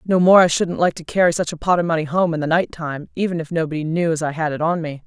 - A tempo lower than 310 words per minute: No, fast, 320 wpm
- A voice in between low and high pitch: Yes, medium, 165 Hz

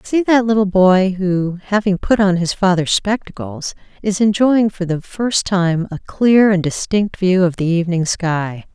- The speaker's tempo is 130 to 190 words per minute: Yes, average, 180 wpm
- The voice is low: No, high, 190 Hz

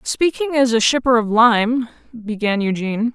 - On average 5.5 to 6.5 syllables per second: No, 4.6 syllables/s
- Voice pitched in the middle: No, high, 235 Hz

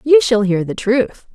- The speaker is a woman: Yes, female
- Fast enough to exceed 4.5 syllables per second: No, 4.1 syllables/s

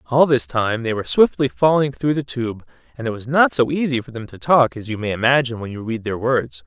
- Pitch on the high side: No, low, 125 Hz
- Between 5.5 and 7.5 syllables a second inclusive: Yes, 5.8 syllables/s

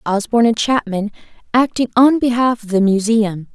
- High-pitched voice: Yes, high, 225 Hz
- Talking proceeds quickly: No, average, 150 wpm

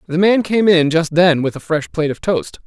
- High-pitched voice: No, medium, 160 Hz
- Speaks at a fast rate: Yes, fast, 270 wpm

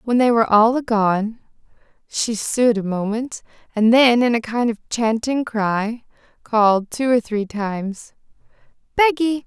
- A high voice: Yes, high, 230 Hz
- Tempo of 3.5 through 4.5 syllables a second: Yes, 4.0 syllables/s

